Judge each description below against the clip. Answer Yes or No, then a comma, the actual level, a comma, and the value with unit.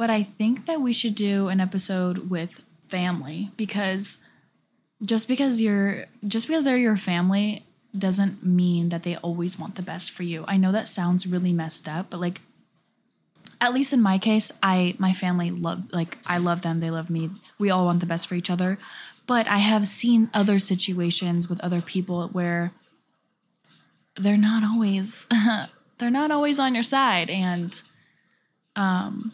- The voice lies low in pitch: No, high, 190 Hz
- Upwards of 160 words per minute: Yes, average, 170 wpm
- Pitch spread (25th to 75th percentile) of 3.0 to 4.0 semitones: Yes, average, 3.7 semitones